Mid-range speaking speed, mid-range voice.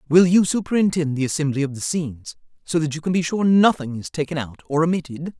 No: fast, 225 wpm; medium, 160 Hz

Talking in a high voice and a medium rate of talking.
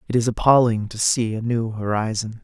No: low, 115 Hz; average, 195 wpm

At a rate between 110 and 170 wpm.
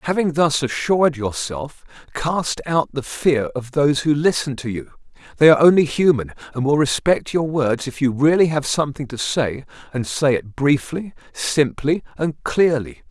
Yes: average, 165 wpm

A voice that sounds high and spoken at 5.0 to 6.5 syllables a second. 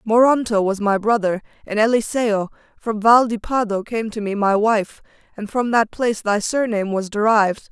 Yes: high, 215 Hz; 5.1 syllables/s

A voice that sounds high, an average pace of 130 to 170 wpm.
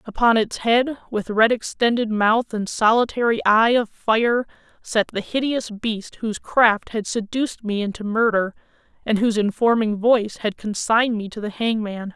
Yes: high, 220 Hz; average, 165 wpm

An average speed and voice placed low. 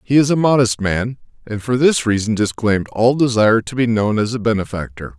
No: fast, 210 wpm; low, 115 Hz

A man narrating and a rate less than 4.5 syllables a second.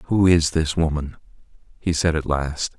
Yes: male; 4.3 syllables/s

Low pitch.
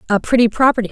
No: high, 230 Hz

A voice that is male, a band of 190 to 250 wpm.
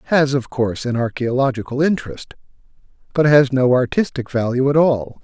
No: male; average, 150 wpm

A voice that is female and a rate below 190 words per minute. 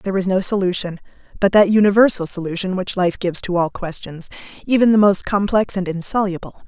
Yes: female; average, 180 wpm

